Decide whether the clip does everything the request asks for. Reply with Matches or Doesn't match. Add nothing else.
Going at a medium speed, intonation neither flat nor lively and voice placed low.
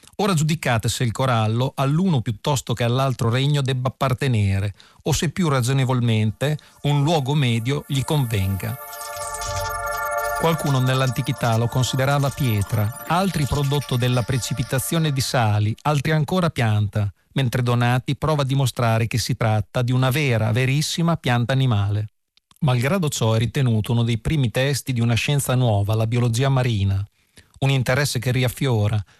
Matches